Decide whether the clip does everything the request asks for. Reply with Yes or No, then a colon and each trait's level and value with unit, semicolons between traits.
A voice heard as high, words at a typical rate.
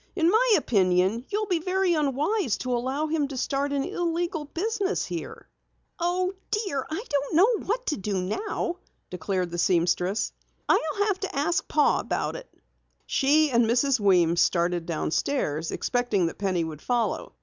Yes: very high, 280 Hz; average, 160 wpm